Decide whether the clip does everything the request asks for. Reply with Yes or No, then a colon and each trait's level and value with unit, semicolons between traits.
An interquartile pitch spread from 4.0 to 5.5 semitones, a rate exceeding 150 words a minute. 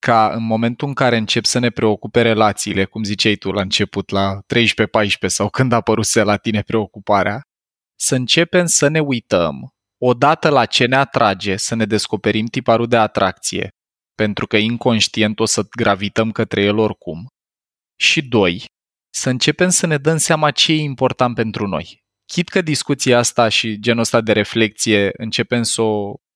No: average, 3.4 semitones; average, 165 wpm